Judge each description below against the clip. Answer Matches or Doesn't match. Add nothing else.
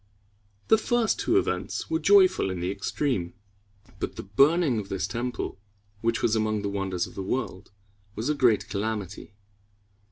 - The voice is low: Matches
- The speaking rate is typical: Matches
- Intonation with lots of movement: Matches